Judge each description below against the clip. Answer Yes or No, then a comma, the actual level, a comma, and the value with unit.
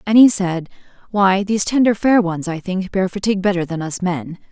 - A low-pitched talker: No, high, 190 Hz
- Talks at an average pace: No, fast, 215 wpm